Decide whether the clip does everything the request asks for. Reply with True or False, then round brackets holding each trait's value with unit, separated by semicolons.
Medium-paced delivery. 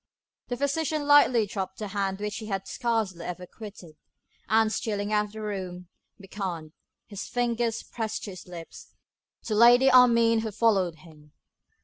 True (155 wpm)